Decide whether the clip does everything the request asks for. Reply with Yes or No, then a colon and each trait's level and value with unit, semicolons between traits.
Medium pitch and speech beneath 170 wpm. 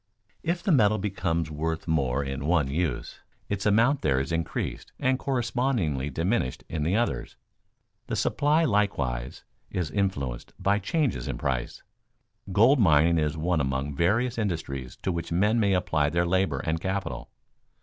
No: very low, 85 Hz; average, 150 wpm